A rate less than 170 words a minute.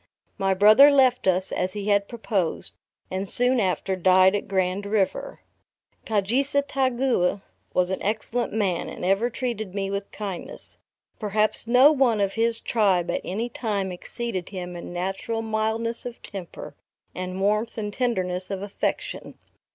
Yes: average, 145 wpm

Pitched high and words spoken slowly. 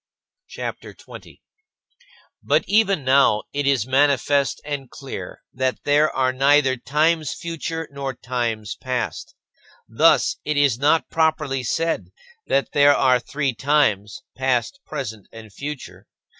No: medium, 140 Hz; slow, 130 wpm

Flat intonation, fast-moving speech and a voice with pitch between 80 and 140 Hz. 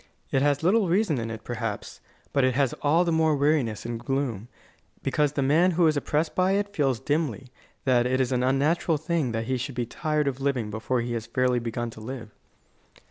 No: average, 4.4 semitones; fast, 210 wpm; low, 135 Hz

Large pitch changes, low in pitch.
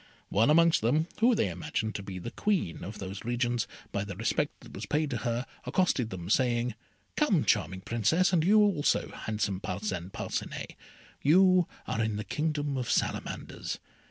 Yes: wide, 7.3 semitones; low, 120 Hz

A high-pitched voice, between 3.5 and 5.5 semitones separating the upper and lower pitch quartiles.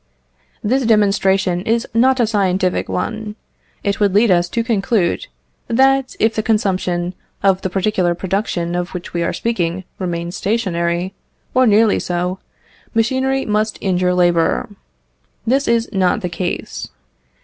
Yes: high, 195 Hz; average, 4.0 semitones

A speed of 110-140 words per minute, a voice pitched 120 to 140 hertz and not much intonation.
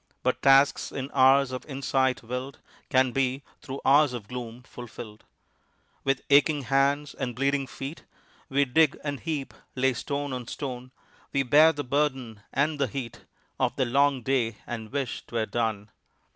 No: average, 160 wpm; low, 135 Hz; narrow, 2.2 semitones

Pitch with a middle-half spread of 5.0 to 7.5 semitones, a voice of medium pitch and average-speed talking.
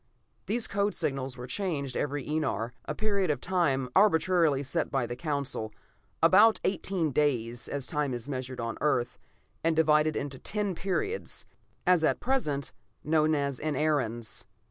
Yes: wide, 5.4 semitones; medium, 150 Hz; average, 150 wpm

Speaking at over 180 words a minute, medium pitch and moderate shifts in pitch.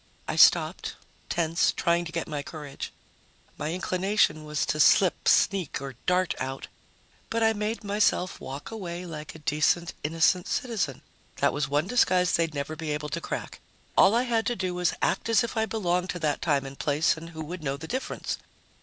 Yes: average, 190 wpm; medium, 170 Hz; average, 4.1 semitones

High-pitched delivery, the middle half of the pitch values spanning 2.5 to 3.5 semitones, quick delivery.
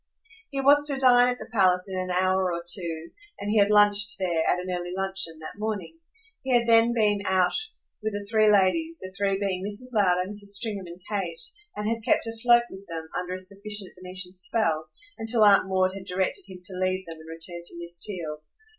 Yes: high, 195 Hz; average, 3.1 semitones; fast, 210 wpm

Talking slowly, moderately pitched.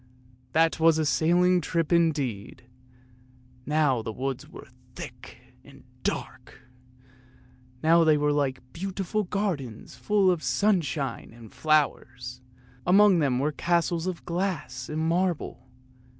Yes: slow, 120 wpm; medium, 160 Hz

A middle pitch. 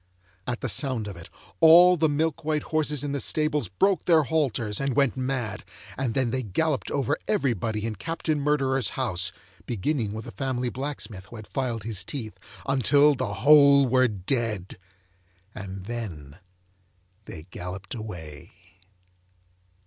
No: low, 130 Hz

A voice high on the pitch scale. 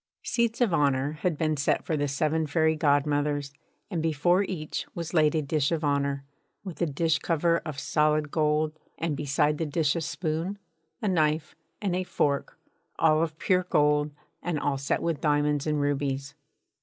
No: medium, 155 Hz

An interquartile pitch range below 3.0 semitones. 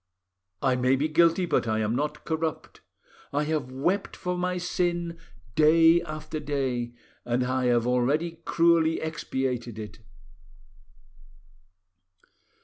No: average, 4.8 semitones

